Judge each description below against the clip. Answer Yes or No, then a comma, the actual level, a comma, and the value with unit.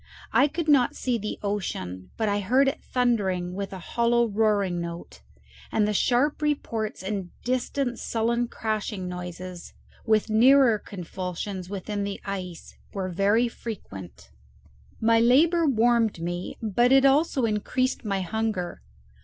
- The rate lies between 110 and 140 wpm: Yes, slow, 135 wpm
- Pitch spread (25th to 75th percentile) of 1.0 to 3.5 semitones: No, average, 4.5 semitones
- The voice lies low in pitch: No, high, 215 Hz